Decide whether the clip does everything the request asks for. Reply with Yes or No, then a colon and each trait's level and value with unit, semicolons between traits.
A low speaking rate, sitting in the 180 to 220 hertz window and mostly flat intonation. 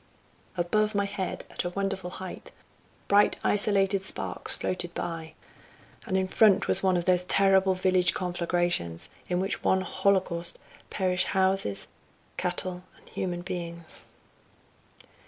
Yes: slow, 130 wpm; medium, 185 Hz; narrow, 1.7 semitones